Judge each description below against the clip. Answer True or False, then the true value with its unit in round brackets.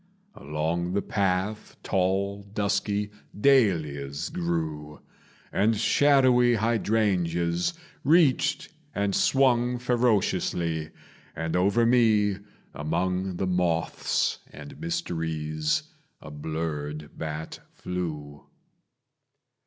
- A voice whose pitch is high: False (90 Hz)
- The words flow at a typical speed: False (80 wpm)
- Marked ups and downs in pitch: True (5.7 semitones)